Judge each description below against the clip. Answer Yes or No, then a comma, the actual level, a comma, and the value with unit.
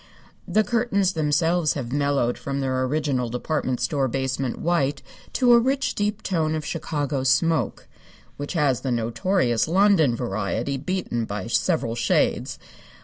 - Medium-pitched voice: Yes, medium, 145 Hz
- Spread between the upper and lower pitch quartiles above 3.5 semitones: Yes, wide, 5.4 semitones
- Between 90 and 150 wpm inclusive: Yes, average, 140 wpm